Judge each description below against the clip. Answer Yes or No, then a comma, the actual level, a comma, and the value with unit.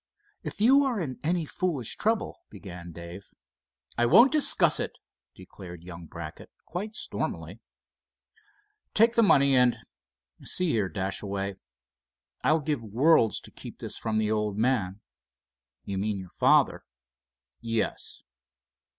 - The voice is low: Yes, low, 110 Hz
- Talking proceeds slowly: Yes, slow, 125 wpm